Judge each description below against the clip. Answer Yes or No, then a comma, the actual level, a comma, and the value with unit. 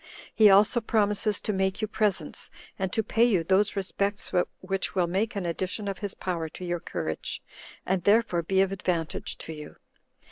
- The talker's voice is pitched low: No, high, 190 Hz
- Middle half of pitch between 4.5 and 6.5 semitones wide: No, average, 2.9 semitones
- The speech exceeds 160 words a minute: Yes, average, 180 wpm